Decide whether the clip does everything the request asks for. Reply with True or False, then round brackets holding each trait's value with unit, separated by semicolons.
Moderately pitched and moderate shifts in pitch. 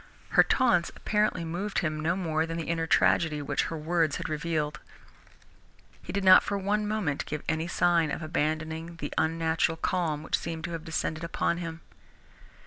False (165 Hz; 1.7 semitones)